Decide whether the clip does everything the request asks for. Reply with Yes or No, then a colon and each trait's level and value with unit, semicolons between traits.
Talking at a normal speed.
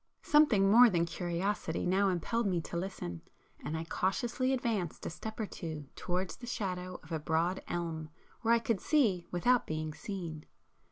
Yes: average, 170 wpm